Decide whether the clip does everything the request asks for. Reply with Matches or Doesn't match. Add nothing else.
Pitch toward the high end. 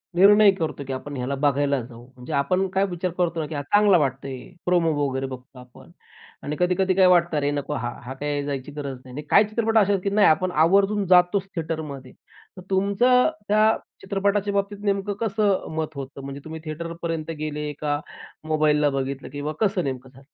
Doesn't match